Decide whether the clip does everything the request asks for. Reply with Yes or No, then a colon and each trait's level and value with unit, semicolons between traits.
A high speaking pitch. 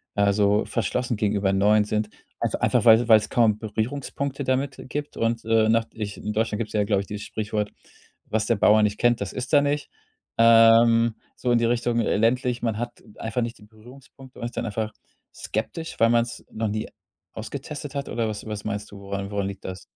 No: low, 110 Hz